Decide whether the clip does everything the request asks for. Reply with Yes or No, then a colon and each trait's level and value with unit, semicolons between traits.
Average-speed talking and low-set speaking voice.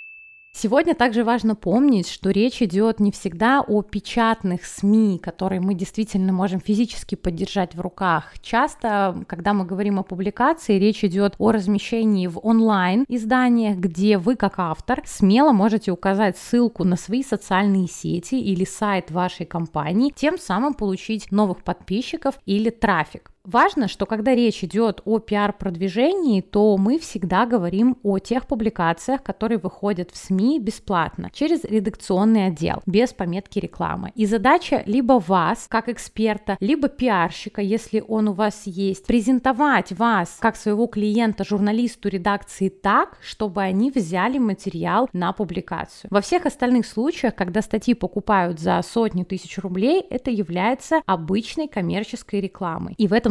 No: average, 145 wpm; high, 210 Hz